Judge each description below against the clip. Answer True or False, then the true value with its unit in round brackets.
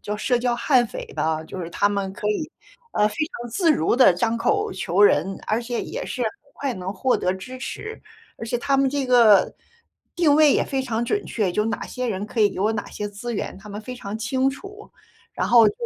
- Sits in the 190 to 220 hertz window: False (230 Hz)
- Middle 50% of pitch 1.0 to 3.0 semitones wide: False (4.3 semitones)